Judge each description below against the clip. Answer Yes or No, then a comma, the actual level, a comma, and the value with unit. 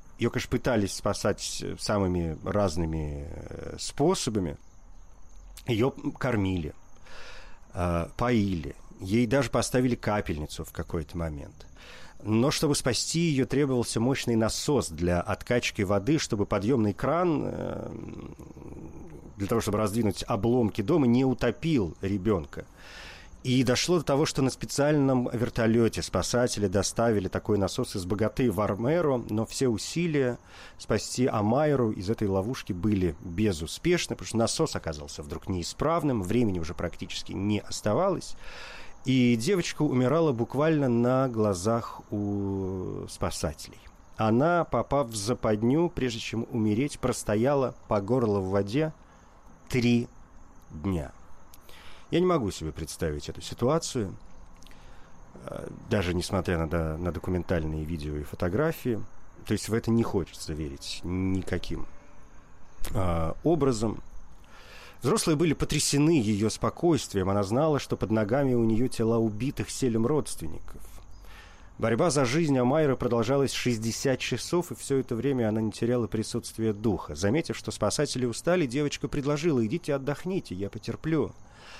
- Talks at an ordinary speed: Yes, average, 120 wpm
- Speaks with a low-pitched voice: Yes, low, 110 Hz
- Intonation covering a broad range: Yes, wide, 5.9 semitones